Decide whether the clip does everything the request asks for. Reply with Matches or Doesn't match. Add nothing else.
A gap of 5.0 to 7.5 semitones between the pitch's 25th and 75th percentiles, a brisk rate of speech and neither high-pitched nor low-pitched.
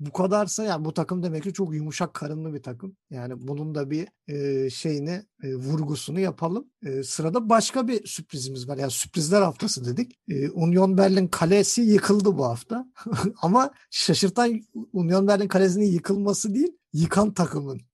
Matches